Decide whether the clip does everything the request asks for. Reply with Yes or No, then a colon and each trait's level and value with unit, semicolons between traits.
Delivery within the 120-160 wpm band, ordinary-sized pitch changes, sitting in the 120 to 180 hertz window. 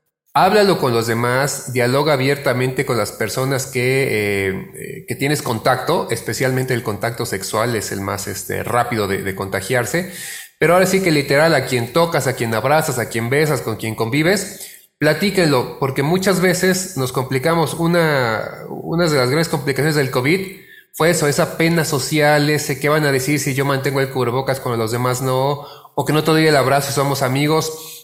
No: average, 180 wpm; average, 4.3 semitones; medium, 140 Hz